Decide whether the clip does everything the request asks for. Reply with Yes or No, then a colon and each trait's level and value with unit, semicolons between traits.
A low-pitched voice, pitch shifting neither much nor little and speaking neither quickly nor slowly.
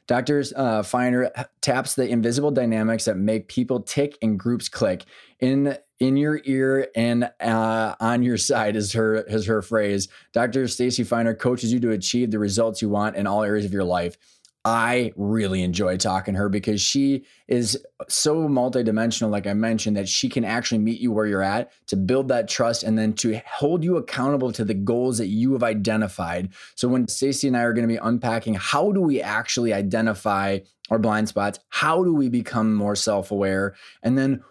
Yes: low, 115 Hz; average, 3.0 semitones; average, 195 wpm